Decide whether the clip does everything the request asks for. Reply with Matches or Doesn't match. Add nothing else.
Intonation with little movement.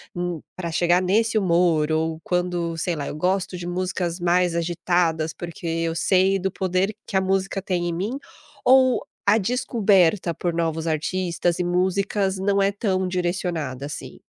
Matches